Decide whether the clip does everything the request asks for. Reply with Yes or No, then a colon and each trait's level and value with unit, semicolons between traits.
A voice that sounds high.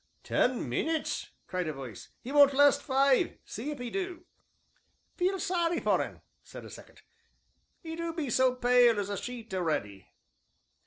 Yes: very high, 260 Hz